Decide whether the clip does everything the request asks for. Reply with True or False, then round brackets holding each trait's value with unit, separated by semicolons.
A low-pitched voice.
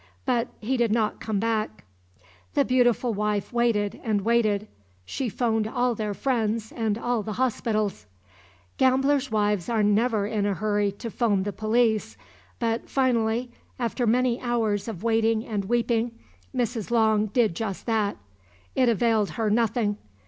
False (225 Hz)